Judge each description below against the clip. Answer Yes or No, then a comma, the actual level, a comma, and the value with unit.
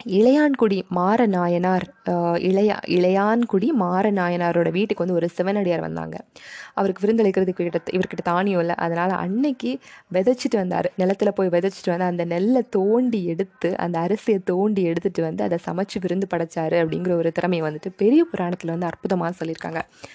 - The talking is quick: Yes, fast, 135 wpm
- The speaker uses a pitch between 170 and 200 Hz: Yes, medium, 185 Hz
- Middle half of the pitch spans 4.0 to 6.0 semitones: No, average, 3.1 semitones